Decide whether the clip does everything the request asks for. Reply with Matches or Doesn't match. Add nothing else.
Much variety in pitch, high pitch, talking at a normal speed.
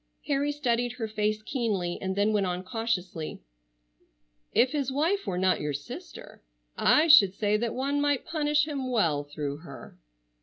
Matches